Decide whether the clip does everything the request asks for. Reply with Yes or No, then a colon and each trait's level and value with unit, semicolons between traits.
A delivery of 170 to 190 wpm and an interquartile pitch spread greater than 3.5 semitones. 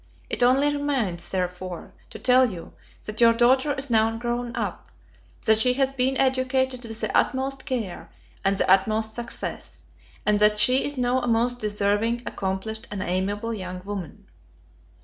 No: average, 160 wpm; average, 3.9 semitones